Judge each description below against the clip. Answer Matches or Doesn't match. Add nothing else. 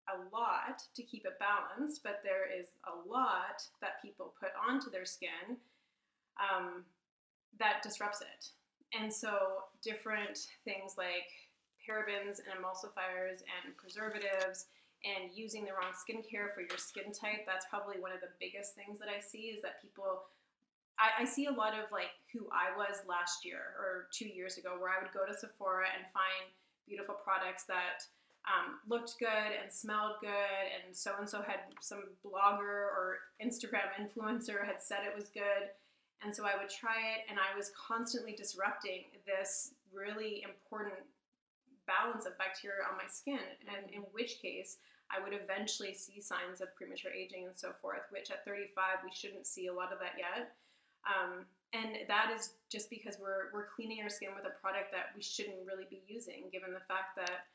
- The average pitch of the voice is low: Doesn't match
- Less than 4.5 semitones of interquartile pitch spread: Matches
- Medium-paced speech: Matches